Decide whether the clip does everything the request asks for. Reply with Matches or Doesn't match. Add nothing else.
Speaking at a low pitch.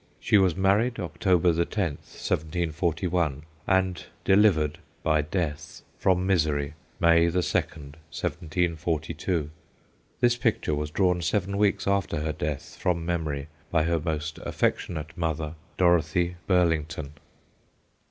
Matches